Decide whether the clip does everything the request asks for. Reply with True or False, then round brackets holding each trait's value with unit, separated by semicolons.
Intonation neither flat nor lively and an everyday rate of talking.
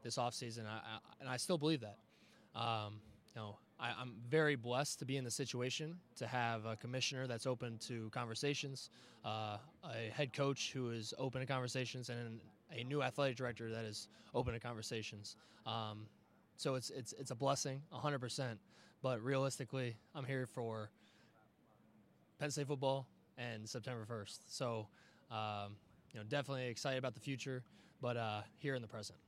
True (3.4 semitones; 165 wpm)